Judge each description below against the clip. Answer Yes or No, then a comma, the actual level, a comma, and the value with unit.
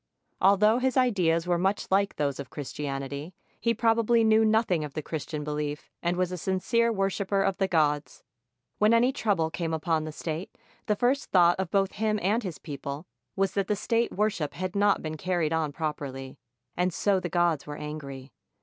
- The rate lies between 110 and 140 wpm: No, average, 190 wpm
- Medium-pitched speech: Yes, medium, 180 Hz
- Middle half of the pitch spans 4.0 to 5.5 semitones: Yes, average, 5.2 semitones